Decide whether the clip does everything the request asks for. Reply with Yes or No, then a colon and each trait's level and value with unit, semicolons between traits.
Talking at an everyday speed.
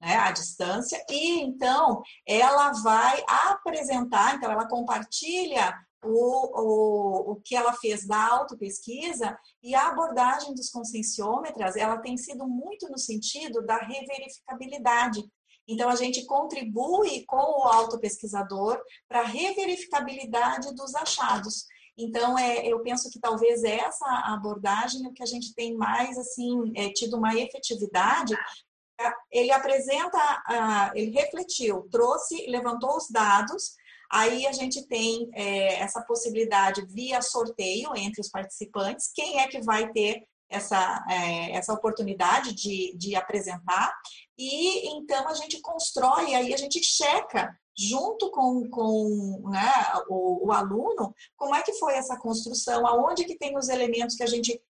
Yes: average, 135 wpm